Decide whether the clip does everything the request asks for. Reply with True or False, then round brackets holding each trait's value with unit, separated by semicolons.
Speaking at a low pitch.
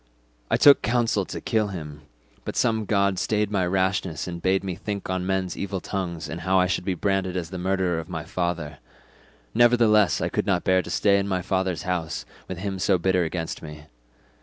True (95 Hz)